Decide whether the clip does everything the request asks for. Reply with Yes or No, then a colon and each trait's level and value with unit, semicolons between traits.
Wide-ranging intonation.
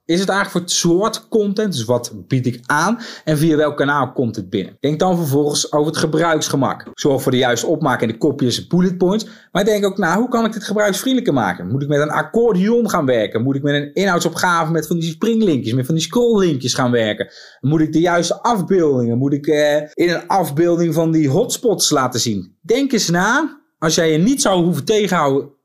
Yes: wide, 5.8 semitones